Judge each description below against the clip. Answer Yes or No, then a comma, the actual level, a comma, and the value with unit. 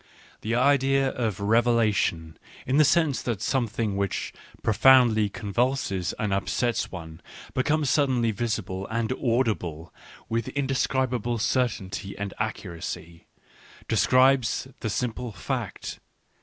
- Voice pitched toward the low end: Yes, low, 115 Hz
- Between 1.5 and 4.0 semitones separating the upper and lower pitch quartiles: No, average, 4.5 semitones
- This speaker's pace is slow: Yes, slow, 115 wpm